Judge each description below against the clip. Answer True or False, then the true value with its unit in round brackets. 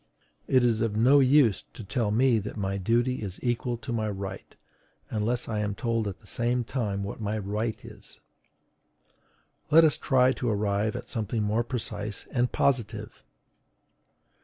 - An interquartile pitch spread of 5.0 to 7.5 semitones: False (2.9 semitones)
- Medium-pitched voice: False (115 Hz)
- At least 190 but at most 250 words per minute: False (160 wpm)